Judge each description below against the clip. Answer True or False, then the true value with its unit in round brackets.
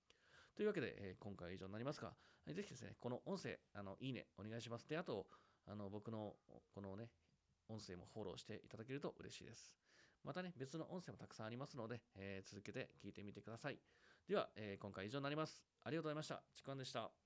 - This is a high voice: False (110 Hz)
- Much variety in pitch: True (5.9 semitones)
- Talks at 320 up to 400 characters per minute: False (425 characters per minute)